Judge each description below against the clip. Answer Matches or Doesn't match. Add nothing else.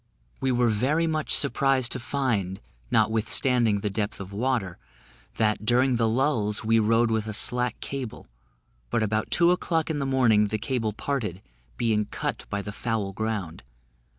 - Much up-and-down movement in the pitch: Doesn't match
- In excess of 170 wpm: Doesn't match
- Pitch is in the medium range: Doesn't match